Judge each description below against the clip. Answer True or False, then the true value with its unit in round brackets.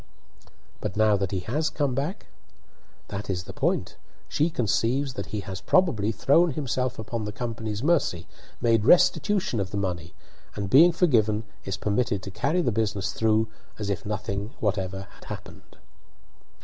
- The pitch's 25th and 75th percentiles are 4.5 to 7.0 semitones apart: True (5.2 semitones)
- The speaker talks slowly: False (160 wpm)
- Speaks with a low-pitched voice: True (110 Hz)